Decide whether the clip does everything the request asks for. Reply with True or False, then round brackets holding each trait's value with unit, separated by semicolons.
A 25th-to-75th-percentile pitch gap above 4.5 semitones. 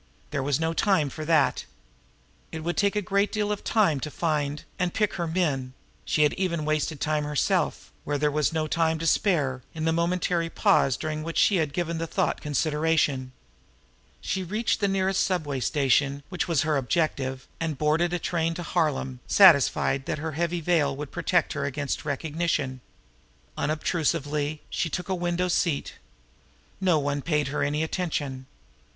False (3.2 semitones)